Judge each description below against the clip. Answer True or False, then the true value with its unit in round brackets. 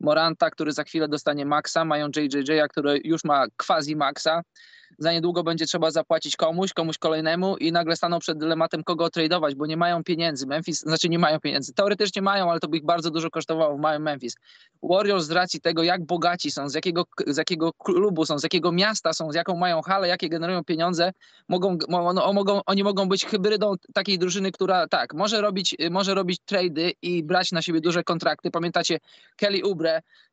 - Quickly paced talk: True (195 wpm)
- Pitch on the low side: False (170 Hz)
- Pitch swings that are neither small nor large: False (2.3 semitones)